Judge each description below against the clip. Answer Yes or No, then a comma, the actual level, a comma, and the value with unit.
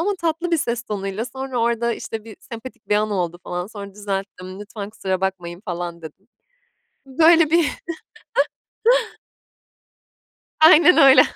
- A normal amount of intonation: No, wide, 5.7 semitones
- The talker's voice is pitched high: Yes, high, 215 Hz